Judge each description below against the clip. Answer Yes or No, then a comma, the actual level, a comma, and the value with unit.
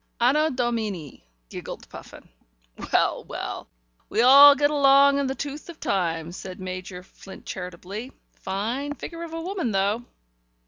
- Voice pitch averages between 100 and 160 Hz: No, high, 240 Hz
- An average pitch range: No, wide, 7.1 semitones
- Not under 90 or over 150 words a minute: Yes, average, 140 wpm